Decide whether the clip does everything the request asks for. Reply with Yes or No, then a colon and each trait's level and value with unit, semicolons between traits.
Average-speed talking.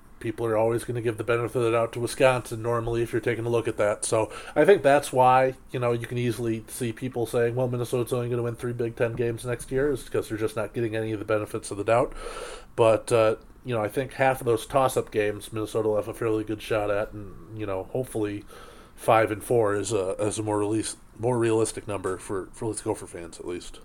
No: fast, 255 wpm